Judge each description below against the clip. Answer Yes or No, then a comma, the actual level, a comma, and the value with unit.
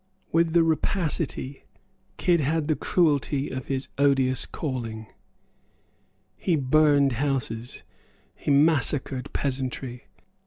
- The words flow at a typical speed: No, slow, 100 wpm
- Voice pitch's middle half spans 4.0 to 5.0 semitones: No, average, 3.1 semitones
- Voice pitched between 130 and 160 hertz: Yes, medium, 140 Hz